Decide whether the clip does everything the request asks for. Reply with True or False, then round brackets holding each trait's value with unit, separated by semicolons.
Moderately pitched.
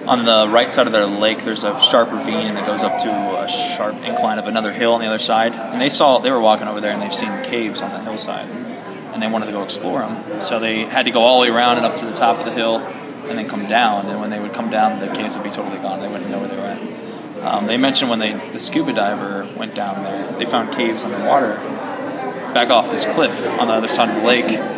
False (110 Hz)